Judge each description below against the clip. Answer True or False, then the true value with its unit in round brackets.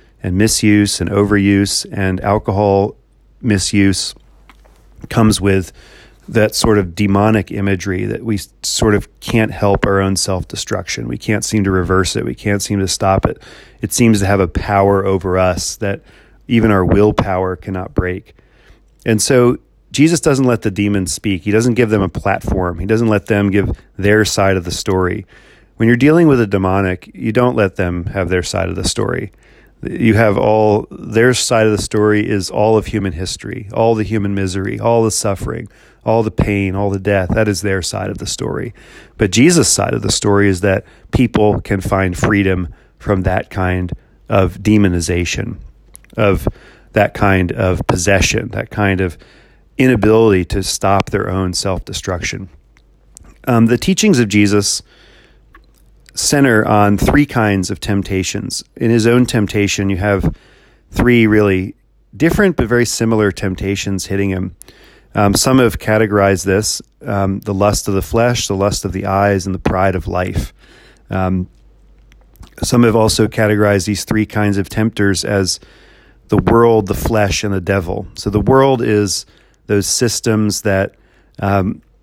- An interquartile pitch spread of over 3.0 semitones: False (2.5 semitones)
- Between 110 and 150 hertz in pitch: False (100 Hz)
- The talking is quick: False (165 wpm)